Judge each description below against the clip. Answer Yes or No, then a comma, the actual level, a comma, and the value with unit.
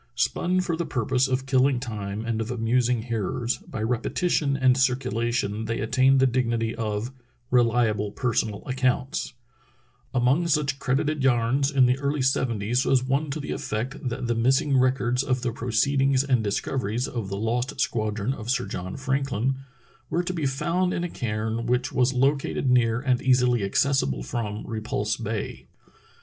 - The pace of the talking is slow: No, average, 165 wpm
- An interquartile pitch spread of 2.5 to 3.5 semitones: Yes, average, 2.9 semitones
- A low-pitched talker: Yes, low, 125 Hz